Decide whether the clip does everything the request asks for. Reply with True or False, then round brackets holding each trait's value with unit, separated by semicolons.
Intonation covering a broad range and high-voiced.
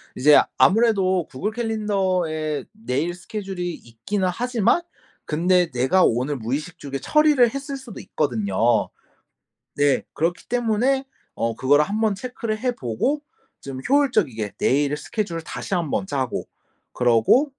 False (8.1 semitones; 180 Hz)